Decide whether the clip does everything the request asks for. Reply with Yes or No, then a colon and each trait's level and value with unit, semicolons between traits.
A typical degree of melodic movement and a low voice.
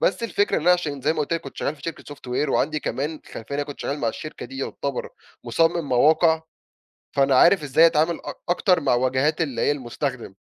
No: average, 3.4 semitones; medium, 145 Hz